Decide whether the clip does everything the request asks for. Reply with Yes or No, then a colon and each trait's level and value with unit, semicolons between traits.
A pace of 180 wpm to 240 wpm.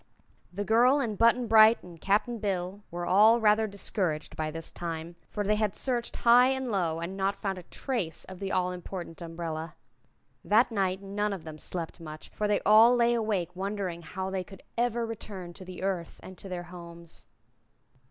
Yes: average, 190 wpm